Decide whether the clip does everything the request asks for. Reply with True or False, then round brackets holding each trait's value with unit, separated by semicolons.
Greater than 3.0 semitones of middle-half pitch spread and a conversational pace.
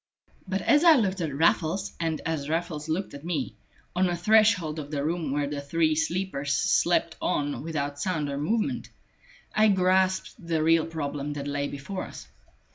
True (4.3 semitones; 175 wpm)